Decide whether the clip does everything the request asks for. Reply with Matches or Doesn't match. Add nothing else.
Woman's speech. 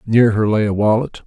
Doesn't match